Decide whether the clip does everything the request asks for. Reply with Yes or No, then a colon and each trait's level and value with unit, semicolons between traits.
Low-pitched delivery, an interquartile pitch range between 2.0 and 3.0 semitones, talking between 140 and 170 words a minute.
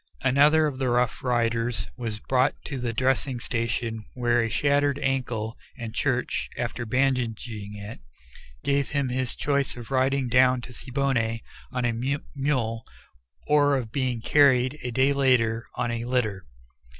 Yes: low, 125 Hz; average, 2.7 semitones; average, 150 wpm